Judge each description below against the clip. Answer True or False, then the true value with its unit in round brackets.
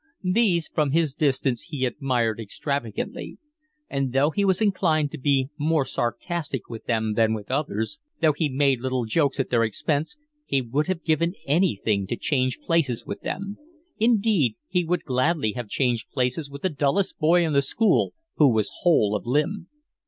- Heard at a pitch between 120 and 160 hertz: True (140 Hz)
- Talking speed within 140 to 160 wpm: False (175 wpm)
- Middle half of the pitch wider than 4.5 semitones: True (5.2 semitones)